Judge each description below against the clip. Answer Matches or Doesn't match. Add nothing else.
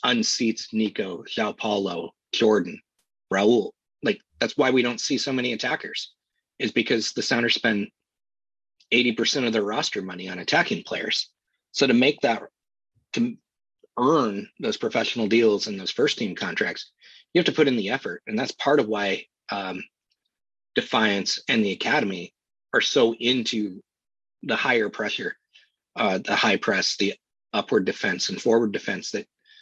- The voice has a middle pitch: Doesn't match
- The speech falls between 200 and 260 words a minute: Doesn't match